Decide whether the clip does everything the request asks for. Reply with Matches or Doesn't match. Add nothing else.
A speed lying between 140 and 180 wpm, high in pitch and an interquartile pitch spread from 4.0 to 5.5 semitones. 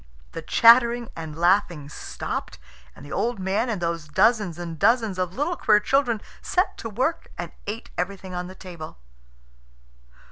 Matches